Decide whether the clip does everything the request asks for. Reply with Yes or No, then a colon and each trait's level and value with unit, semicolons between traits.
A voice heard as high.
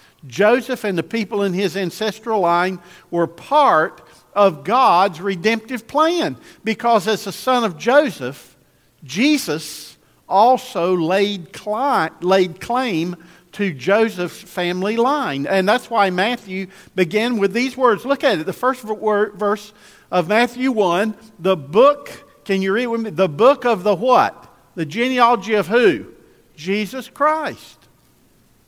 Yes: high, 210 Hz